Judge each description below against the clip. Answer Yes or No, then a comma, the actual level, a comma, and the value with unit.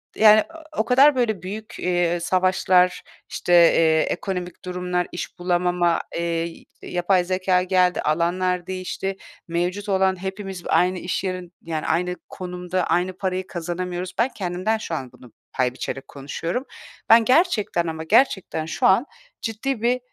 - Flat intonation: Yes, narrow, 1.8 semitones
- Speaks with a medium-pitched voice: Yes, medium, 180 Hz